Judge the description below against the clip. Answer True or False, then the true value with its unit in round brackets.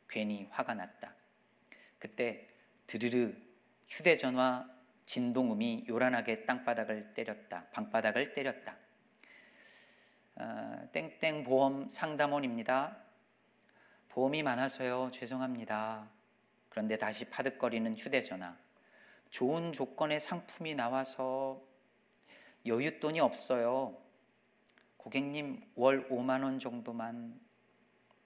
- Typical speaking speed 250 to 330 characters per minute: False (215 characters per minute)